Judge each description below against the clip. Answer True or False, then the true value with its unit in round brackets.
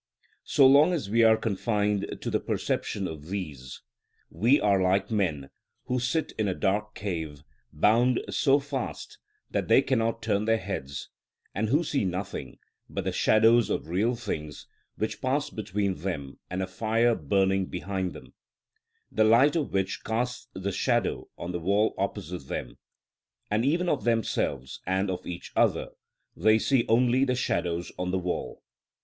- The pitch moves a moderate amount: True (4.3 semitones)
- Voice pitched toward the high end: False (105 Hz)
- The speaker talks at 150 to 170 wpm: True (160 wpm)